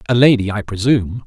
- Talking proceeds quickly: No, average, 190 wpm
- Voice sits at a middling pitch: No, low, 110 Hz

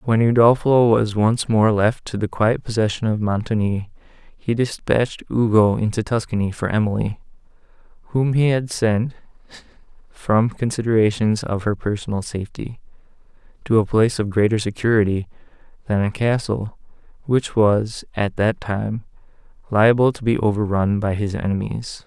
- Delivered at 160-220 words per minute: No, slow, 135 wpm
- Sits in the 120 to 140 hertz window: No, low, 110 Hz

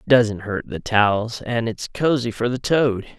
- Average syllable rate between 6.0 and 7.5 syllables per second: No, 4.3 syllables/s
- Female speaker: No, male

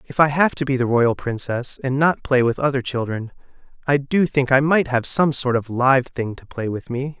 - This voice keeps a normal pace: No, fast, 240 wpm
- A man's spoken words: Yes, male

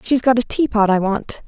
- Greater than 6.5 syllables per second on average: No, 5.1 syllables/s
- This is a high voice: Yes, high, 225 Hz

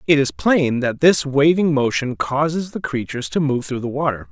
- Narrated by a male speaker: Yes, male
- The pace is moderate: No, fast, 210 wpm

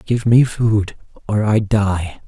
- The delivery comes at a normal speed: Yes, average, 160 wpm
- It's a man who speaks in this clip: Yes, male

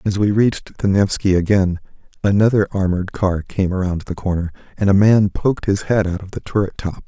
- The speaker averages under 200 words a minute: No, fast, 205 wpm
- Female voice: No, male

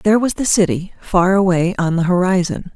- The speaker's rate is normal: Yes, average, 195 wpm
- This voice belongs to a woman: Yes, female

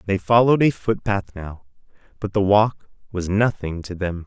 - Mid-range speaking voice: No, low, 100 Hz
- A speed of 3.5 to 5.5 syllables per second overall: Yes, 4.8 syllables/s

